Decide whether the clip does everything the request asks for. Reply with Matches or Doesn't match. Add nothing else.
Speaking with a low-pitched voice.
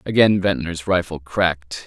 Matches